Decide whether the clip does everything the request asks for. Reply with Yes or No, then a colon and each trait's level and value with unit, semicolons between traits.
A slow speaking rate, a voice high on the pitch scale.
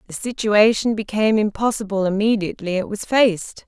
Yes: slow, 130 wpm; high, 210 Hz